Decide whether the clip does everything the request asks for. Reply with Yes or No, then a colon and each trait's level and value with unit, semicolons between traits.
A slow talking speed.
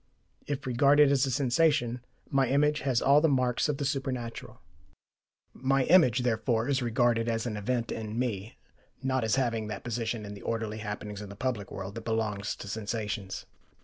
No: average, 180 wpm